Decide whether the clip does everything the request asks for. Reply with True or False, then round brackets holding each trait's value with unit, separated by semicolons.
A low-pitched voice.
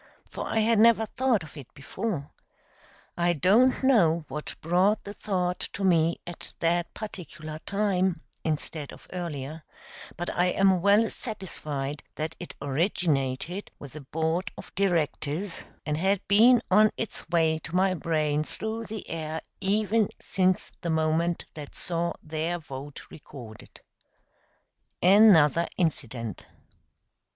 False (170 Hz)